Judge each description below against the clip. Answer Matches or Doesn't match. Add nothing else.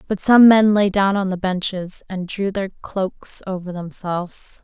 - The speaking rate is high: Doesn't match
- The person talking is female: Matches